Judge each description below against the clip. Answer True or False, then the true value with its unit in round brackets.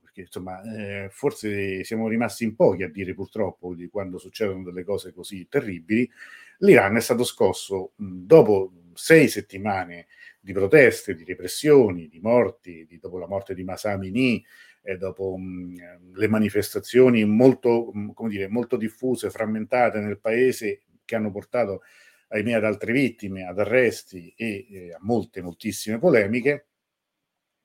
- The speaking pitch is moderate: False (105 Hz)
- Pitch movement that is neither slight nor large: True (3.6 semitones)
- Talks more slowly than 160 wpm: True (145 wpm)